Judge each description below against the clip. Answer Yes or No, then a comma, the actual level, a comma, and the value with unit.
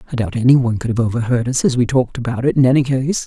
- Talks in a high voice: No, low, 125 Hz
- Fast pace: Yes, fast, 275 wpm